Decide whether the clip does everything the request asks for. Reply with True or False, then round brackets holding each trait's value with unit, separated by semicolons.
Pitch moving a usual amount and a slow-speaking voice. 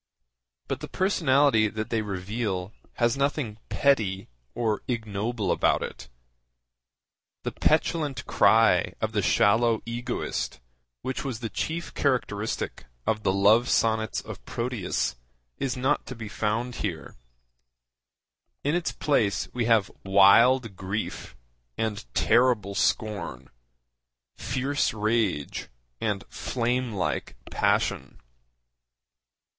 True (3.6 semitones; 110 wpm)